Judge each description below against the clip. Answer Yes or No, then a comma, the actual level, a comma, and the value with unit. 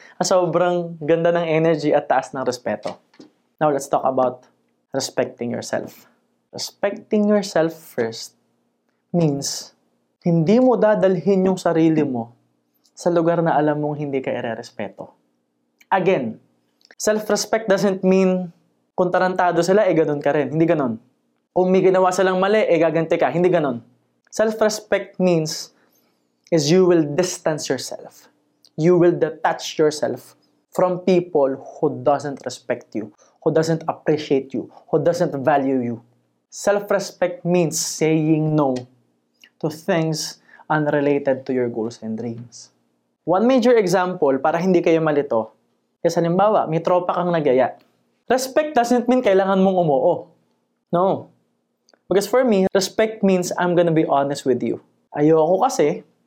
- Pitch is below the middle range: No, medium, 165 Hz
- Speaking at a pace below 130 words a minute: No, average, 135 wpm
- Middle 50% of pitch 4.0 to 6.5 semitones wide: Yes, average, 5.1 semitones